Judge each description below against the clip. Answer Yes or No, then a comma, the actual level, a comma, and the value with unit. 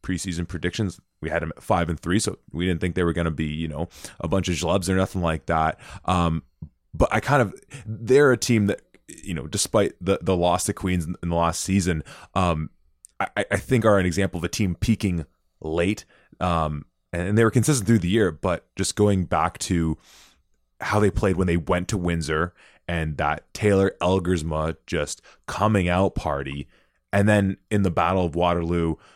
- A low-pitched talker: Yes, very low, 90 Hz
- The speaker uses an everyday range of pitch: Yes, average, 3.4 semitones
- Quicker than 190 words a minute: Yes, average, 200 wpm